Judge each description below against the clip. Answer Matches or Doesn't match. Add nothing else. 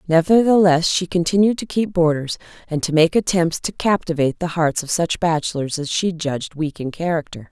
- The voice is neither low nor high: Matches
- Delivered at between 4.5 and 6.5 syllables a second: Matches